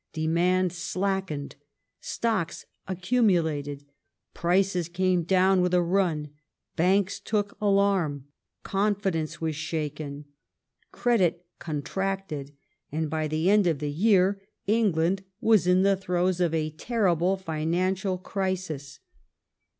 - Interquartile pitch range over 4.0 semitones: No, average, 3.5 semitones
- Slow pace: Yes, slow, 105 wpm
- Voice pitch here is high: No, medium, 180 Hz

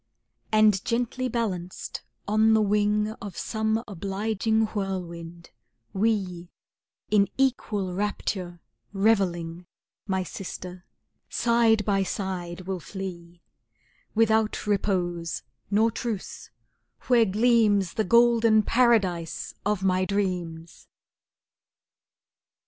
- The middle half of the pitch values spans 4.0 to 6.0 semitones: No, average, 3.3 semitones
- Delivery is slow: Yes, slow, 90 wpm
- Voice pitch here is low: No, high, 200 Hz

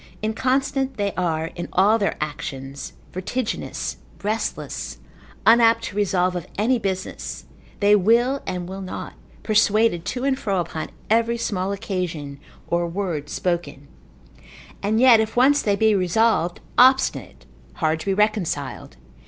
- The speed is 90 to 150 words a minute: Yes, slow, 135 wpm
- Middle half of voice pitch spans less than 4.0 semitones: No, average, 4.7 semitones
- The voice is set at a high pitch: Yes, high, 200 Hz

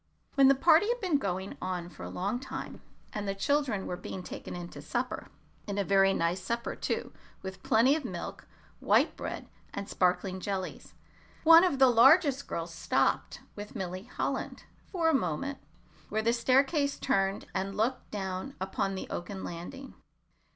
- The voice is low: No, high, 205 Hz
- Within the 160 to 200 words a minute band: Yes, average, 170 wpm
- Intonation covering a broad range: Yes, wide, 6.4 semitones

